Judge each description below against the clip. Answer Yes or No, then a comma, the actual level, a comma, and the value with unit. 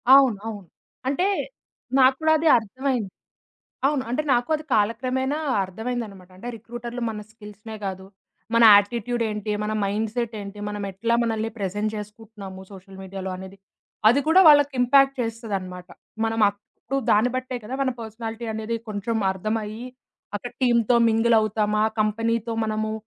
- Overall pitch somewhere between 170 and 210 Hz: No, high, 225 Hz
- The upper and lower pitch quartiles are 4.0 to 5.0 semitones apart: No, average, 2.8 semitones